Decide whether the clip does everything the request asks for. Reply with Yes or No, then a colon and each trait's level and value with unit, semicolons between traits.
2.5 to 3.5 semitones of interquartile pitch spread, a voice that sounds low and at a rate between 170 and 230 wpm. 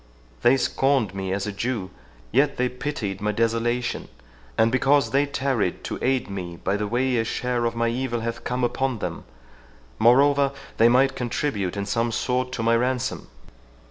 Yes: average, 2.9 semitones; low, 120 Hz; average, 175 wpm